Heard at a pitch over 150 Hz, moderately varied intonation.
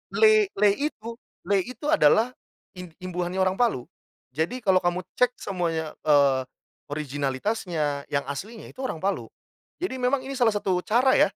No: high, 190 Hz; wide, 7.7 semitones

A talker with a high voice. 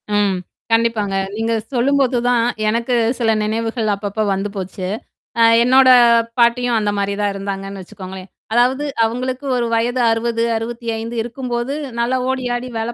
Yes: high, 230 Hz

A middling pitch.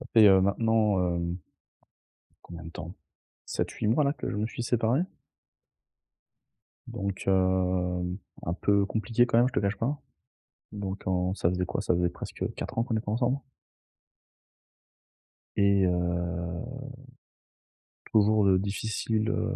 No: low, 100 Hz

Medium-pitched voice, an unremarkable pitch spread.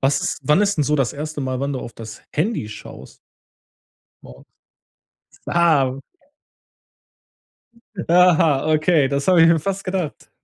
Yes: medium, 150 Hz; average, 4.2 semitones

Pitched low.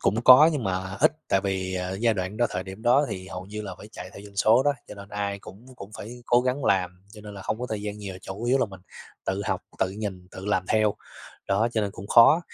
Yes: low, 100 Hz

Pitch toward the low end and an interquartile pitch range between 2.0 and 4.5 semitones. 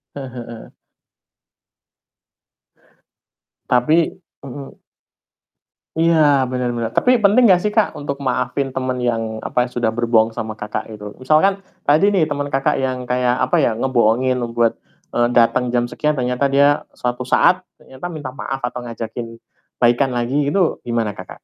Yes: low, 125 Hz; average, 3.4 semitones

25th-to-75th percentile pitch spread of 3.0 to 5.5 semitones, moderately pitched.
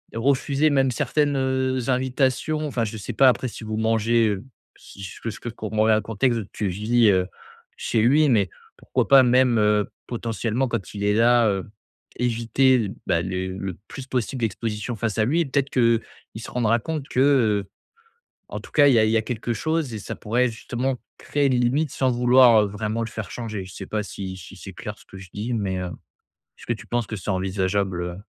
No: average, 3.6 semitones; low, 115 Hz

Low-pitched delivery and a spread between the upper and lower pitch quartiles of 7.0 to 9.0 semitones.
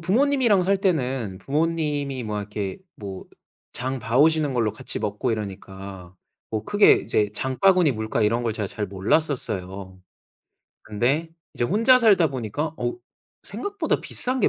Yes: low, 130 Hz; wide, 8.0 semitones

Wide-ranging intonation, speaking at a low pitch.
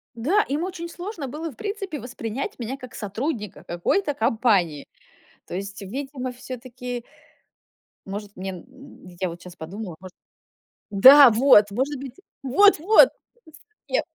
No: wide, 6.2 semitones; very high, 250 Hz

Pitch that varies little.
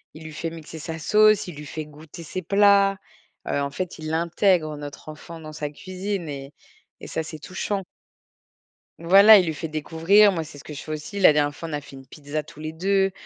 No: average, 3.7 semitones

